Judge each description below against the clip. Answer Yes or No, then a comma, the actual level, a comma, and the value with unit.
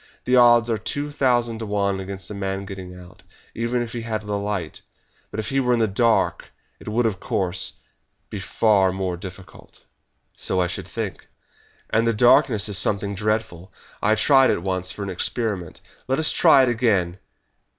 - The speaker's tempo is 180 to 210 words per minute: Yes, average, 185 wpm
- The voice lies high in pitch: No, low, 105 Hz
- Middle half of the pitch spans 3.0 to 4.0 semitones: Yes, average, 3.5 semitones